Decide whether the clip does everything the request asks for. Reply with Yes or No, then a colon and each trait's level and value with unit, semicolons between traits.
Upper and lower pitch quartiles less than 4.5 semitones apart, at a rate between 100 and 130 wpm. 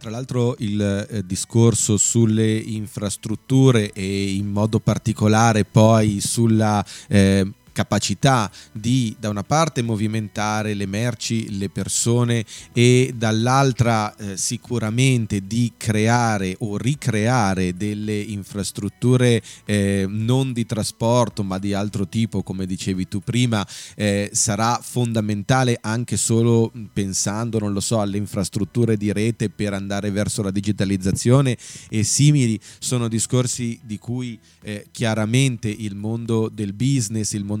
Yes: average, 2.7 semitones; average, 125 wpm